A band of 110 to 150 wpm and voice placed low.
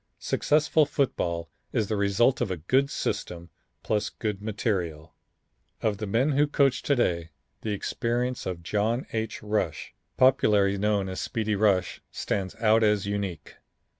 Yes: average, 145 wpm; low, 105 Hz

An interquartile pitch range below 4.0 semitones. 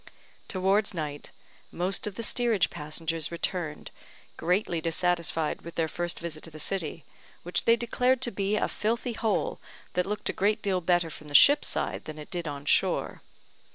No: average, 4.5 semitones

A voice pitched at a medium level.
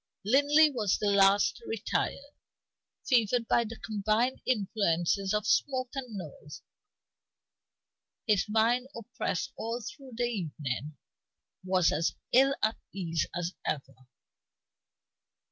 No: high, 215 Hz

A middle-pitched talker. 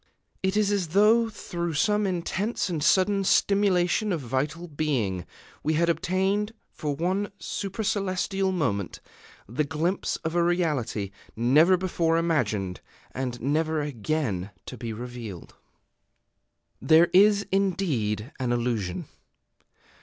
Yes: medium, 165 Hz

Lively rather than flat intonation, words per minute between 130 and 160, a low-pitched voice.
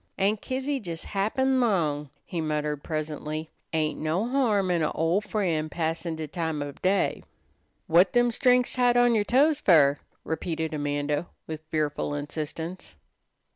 No: wide, 5.7 semitones; average, 145 wpm; medium, 165 Hz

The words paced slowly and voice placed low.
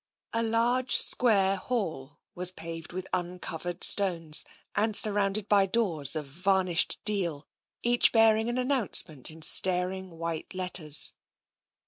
No: slow, 120 wpm; medium, 185 Hz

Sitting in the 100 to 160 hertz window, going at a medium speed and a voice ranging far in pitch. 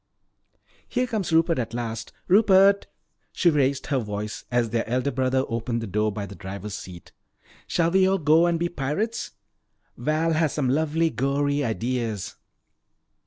Yes: medium, 140 Hz; average, 155 wpm; wide, 6.4 semitones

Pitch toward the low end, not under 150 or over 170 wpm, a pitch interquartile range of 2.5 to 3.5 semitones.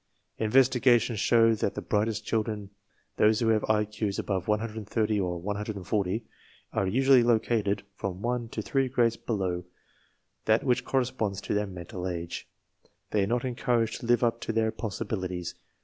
Yes: low, 110 Hz; average, 160 wpm; average, 2.8 semitones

